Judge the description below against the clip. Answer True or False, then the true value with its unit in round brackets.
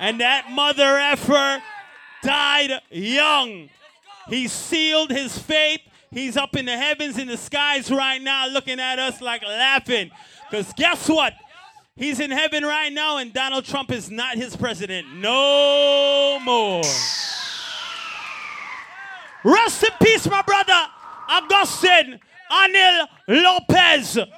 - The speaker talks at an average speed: False (125 wpm)